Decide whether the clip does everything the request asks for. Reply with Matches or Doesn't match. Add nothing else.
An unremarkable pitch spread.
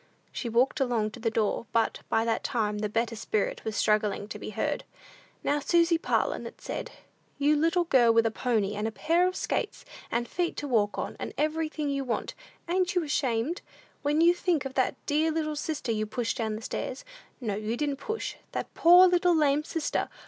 Doesn't match